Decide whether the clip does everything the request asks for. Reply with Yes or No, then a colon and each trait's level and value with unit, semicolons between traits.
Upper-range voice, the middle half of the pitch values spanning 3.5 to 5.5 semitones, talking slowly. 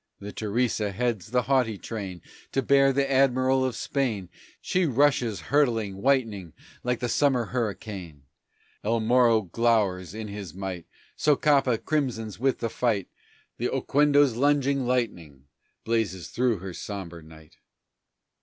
No: low, 115 Hz; average, 4.9 semitones; slow, 130 wpm